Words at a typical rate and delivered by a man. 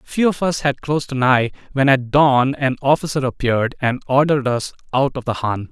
No: fast, 210 wpm; male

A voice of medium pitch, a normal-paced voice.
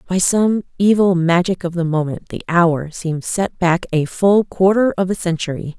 Yes: medium, 175 Hz; average, 185 wpm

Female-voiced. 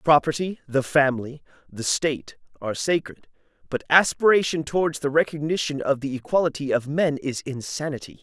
No: male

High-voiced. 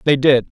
No: low, 135 Hz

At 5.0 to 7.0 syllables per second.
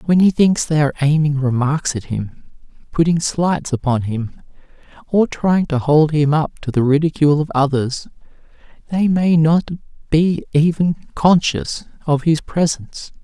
No: 4.5 syllables/s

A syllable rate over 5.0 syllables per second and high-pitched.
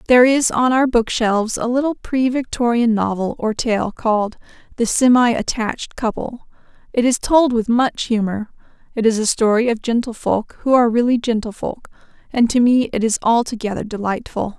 Yes: 5.2 syllables/s; high, 235 Hz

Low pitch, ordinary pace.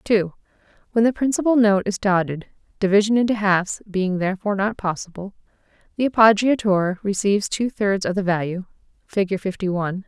No: high, 200 Hz; average, 150 wpm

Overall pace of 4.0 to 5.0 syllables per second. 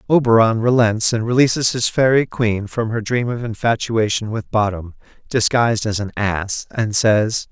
Yes: 4.6 syllables/s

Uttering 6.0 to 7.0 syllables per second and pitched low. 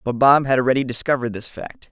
Yes: 6.6 syllables/s; low, 130 Hz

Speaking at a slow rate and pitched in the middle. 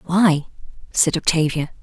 Yes: slow, 100 wpm; medium, 165 Hz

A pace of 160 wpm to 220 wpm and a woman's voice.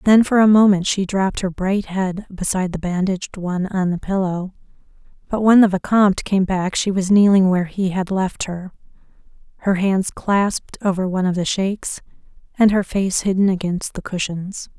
Yes: average, 185 wpm; female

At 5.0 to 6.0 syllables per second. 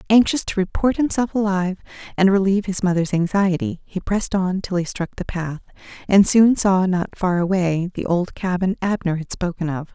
Yes: 5.2 syllables/s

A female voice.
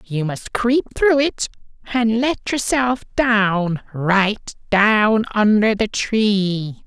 No: male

